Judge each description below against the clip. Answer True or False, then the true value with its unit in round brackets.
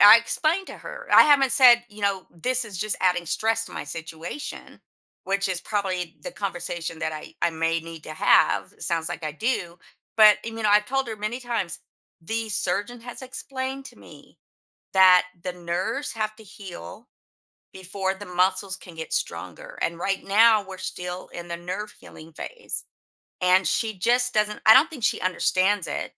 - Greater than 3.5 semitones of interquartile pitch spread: True (4.5 semitones)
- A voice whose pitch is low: False (195 Hz)